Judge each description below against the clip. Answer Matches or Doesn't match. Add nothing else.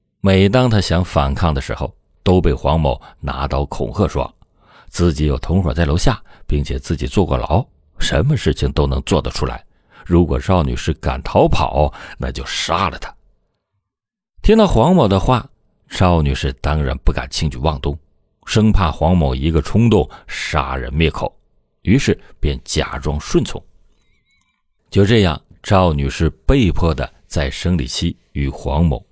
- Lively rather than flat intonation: Doesn't match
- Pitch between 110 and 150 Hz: Doesn't match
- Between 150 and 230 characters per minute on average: Matches